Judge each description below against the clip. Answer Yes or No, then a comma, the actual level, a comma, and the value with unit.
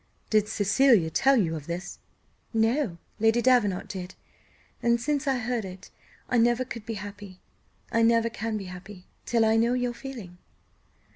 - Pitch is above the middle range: Yes, high, 225 Hz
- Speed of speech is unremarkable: Yes, average, 160 wpm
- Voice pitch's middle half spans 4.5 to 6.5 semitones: No, average, 3.7 semitones